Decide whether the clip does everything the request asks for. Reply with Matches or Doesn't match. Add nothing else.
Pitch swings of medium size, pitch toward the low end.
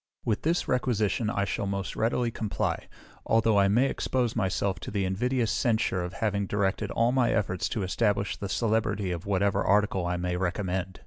Matches